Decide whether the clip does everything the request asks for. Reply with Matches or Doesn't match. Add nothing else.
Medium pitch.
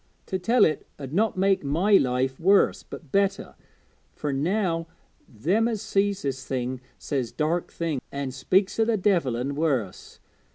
Matches